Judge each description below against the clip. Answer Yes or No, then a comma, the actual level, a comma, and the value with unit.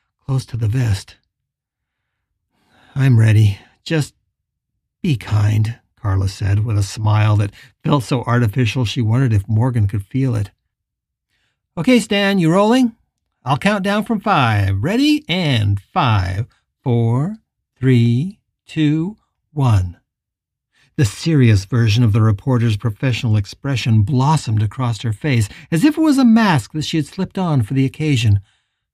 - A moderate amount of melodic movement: No, wide, 6.1 semitones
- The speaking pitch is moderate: No, low, 125 Hz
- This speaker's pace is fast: No, average, 140 wpm